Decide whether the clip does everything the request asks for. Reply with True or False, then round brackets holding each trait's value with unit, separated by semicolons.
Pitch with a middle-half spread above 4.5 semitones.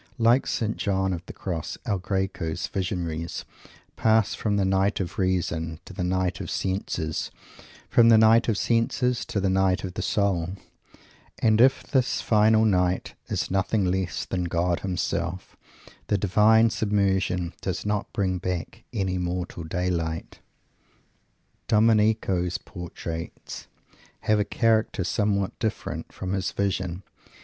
False (3.0 semitones)